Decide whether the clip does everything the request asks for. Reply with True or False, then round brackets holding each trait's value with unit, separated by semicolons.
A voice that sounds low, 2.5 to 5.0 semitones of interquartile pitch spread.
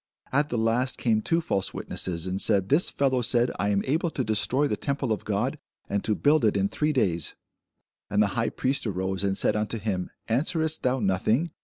False (115 Hz; 5.4 semitones)